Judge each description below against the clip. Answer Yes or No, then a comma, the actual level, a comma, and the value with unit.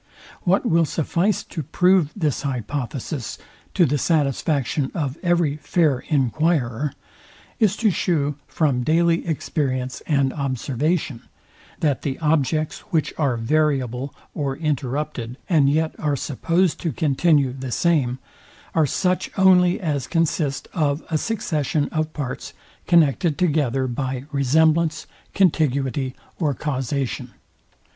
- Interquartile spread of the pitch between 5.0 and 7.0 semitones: No, average, 3.5 semitones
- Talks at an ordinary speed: No, slow, 120 wpm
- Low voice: No, medium, 150 Hz